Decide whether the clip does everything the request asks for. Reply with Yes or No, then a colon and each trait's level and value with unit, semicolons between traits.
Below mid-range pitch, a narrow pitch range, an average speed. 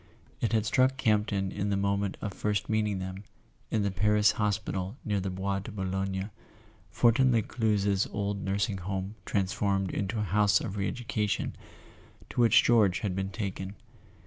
Yes: low, 100 Hz; narrow, 1.7 semitones; average, 165 wpm